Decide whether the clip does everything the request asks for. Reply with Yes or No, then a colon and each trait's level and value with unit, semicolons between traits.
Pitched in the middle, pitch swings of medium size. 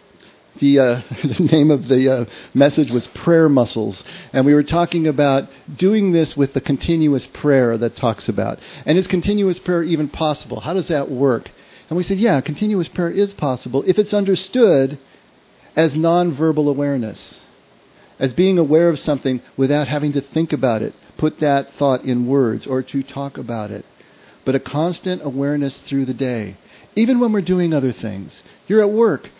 Yes: medium, 145 Hz; average, 4.6 semitones